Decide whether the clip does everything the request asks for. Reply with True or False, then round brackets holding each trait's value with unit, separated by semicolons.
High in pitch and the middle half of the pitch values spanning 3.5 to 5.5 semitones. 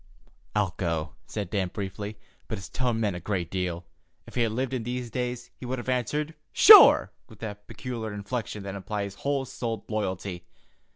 False (105 Hz; 4.1 semitones)